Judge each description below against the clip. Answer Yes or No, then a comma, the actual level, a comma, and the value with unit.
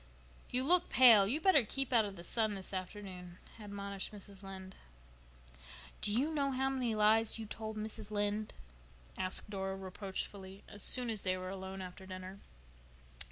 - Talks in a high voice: Yes, high, 205 Hz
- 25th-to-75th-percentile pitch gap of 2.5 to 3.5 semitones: Yes, average, 2.8 semitones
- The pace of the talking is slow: No, average, 160 wpm